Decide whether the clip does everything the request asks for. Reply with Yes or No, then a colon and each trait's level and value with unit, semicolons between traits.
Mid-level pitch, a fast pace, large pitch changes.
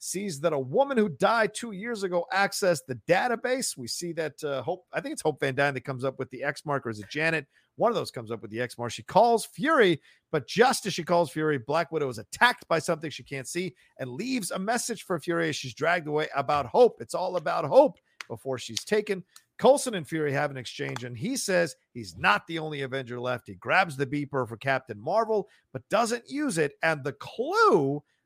Yes: medium, 160 Hz; fast, 230 wpm; wide, 7.4 semitones